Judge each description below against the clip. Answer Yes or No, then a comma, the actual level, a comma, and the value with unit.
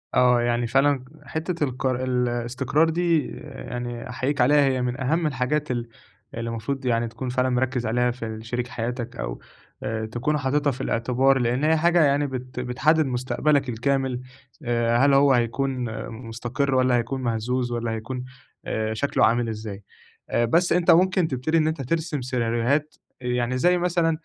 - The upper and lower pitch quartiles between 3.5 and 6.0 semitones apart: No, average, 3.1 semitones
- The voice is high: No, low, 125 Hz